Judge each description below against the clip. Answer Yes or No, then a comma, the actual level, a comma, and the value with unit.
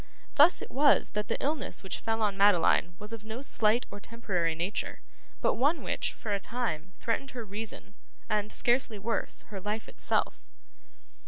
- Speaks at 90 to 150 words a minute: No, average, 170 wpm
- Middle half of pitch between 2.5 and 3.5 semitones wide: Yes, average, 3.1 semitones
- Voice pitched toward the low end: No, high, 215 Hz